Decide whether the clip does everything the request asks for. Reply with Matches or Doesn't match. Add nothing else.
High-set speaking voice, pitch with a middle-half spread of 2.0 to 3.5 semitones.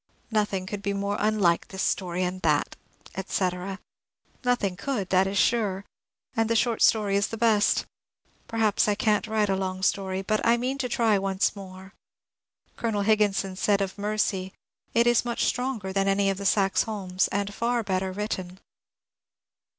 Matches